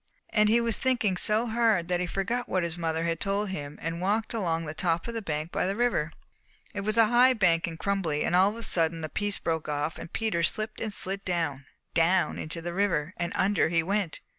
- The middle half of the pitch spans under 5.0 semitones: Yes, average, 4.4 semitones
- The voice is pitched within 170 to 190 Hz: Yes, medium, 185 Hz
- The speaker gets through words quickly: Yes, fast, 235 wpm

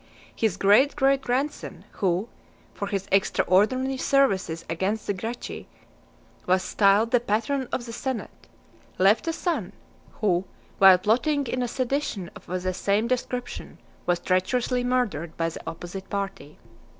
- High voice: Yes, high, 210 Hz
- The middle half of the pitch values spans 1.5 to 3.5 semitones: No, average, 5.3 semitones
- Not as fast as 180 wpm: Yes, average, 140 wpm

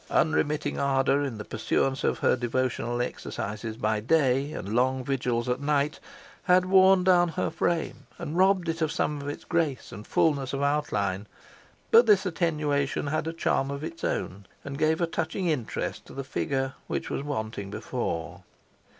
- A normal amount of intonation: Yes, average, 4.6 semitones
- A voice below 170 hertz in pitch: Yes, medium, 140 Hz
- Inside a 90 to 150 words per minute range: No, average, 170 wpm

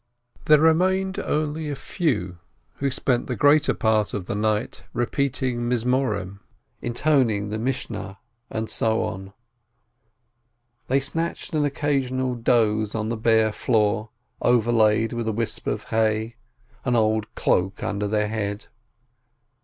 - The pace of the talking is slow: Yes, slow, 130 wpm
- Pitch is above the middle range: No, low, 115 Hz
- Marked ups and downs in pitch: No, average, 3.9 semitones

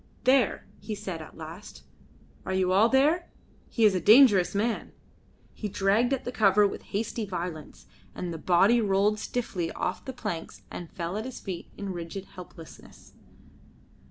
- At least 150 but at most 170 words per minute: Yes, average, 160 wpm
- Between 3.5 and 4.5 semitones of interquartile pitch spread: Yes, average, 4.1 semitones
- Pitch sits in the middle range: No, high, 200 Hz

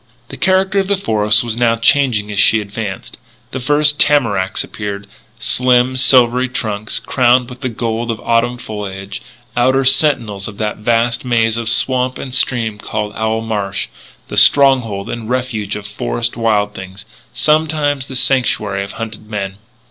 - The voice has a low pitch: Yes, low, 115 Hz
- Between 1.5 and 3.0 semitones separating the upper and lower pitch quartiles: No, average, 3.6 semitones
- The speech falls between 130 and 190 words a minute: Yes, average, 155 wpm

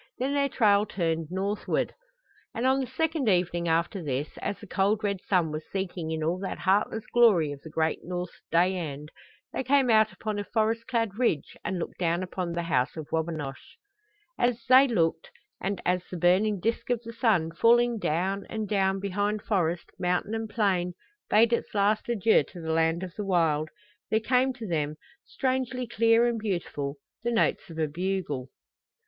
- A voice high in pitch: Yes, high, 195 Hz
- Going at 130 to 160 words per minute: No, average, 185 wpm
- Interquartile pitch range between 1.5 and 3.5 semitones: No, average, 5.2 semitones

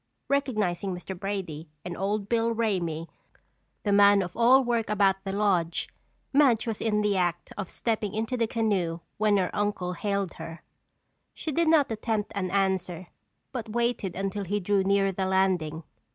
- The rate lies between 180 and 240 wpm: No, average, 165 wpm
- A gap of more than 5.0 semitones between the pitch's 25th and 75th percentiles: No, average, 3.2 semitones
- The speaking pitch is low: No, high, 200 Hz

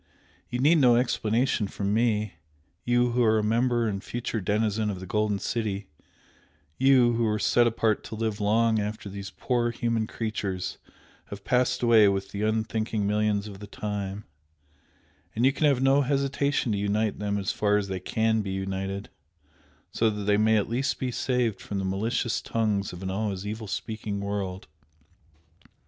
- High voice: No, low, 110 Hz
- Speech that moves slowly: No, average, 175 wpm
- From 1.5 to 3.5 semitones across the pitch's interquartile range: Yes, average, 2.7 semitones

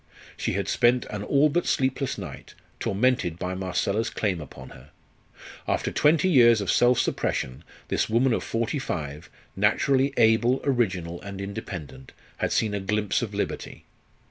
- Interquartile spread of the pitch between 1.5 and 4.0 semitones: No, average, 5.2 semitones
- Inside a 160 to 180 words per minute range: No, average, 150 wpm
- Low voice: Yes, low, 105 Hz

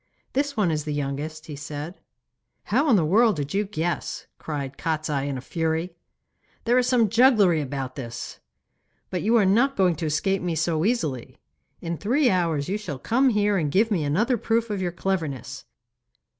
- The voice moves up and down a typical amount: No, wide, 6.0 semitones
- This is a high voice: No, medium, 175 Hz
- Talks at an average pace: Yes, average, 185 wpm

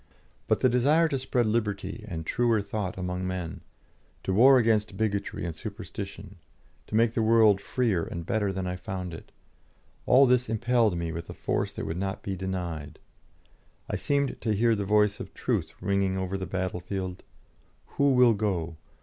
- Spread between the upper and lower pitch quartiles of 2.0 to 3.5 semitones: No, average, 3.9 semitones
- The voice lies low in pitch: Yes, low, 100 Hz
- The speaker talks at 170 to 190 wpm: Yes, average, 175 wpm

